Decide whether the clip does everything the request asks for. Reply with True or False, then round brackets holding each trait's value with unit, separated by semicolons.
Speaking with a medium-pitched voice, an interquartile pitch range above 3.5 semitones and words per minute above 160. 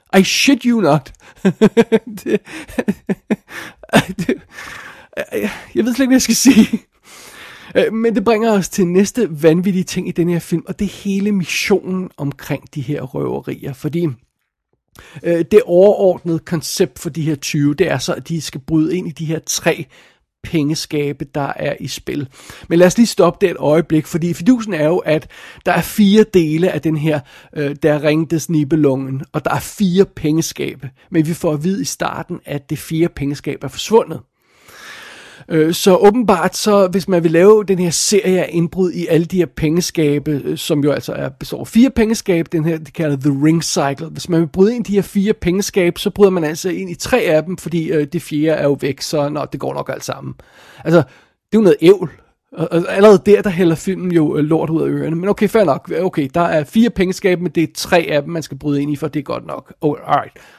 True (170 Hz; 4.1 semitones; 205 wpm)